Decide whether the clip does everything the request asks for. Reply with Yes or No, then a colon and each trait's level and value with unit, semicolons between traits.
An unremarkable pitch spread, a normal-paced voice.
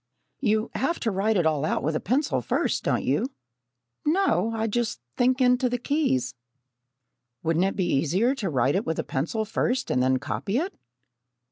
No: wide, 8.1 semitones; average, 180 wpm